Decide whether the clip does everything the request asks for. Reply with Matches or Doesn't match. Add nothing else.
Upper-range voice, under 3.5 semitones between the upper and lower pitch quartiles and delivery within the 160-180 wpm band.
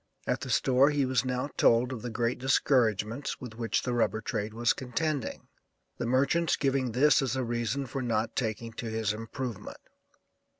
Doesn't match